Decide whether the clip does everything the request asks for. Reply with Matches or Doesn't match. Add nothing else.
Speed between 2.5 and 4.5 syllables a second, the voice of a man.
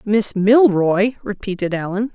Doesn't match